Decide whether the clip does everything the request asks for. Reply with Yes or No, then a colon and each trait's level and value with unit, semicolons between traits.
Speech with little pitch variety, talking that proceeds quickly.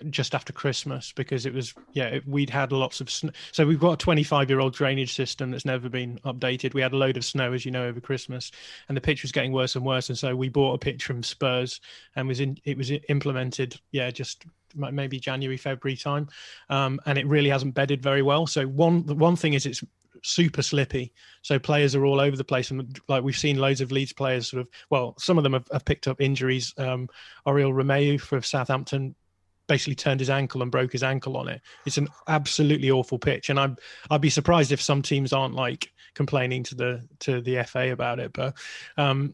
Yes: narrow, 1.6 semitones; fast, 225 wpm